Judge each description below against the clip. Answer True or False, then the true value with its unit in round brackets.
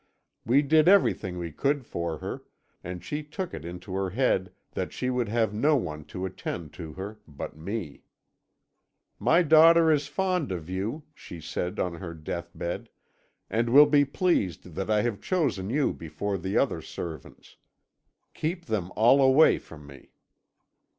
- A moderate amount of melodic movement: False (8.8 semitones)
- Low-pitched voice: True (105 Hz)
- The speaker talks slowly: False (160 wpm)